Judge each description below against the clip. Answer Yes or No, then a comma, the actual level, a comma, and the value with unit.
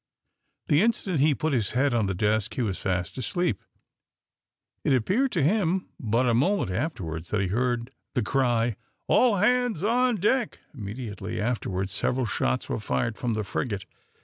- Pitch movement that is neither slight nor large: No, wide, 8.9 semitones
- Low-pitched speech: Yes, low, 125 Hz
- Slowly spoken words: No, average, 165 wpm